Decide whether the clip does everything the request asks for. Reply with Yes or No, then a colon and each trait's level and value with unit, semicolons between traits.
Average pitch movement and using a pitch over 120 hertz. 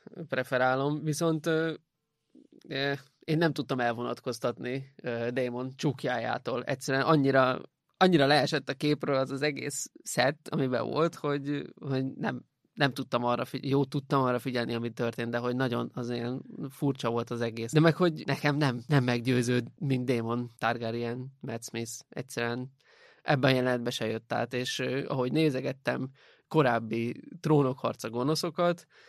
Yes: average, 3.2 semitones; low, 130 Hz